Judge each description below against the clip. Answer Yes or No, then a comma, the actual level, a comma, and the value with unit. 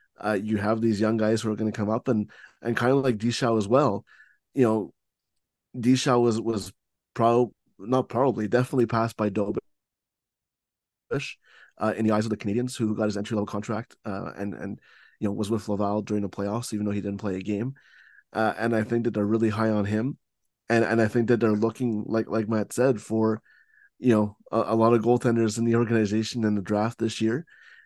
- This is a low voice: Yes, low, 110 Hz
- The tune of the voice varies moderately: No, narrow, 1.8 semitones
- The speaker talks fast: Yes, fast, 215 wpm